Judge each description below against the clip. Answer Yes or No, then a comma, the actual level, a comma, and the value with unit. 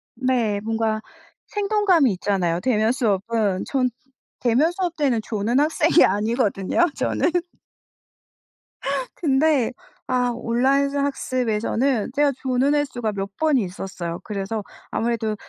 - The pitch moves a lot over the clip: No, average, 4.9 semitones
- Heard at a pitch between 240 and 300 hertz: Yes, high, 245 Hz